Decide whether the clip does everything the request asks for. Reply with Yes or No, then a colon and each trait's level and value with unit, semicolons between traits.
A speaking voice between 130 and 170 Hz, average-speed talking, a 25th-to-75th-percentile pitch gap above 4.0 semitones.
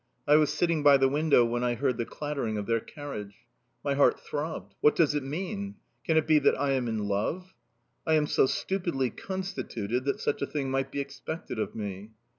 No: medium, 140 Hz; fast, 210 wpm; average, 4.5 semitones